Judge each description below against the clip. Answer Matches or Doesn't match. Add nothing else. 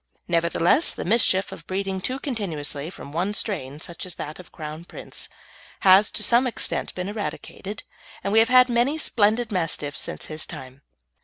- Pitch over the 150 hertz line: Matches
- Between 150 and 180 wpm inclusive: Matches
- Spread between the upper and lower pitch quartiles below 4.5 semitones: Doesn't match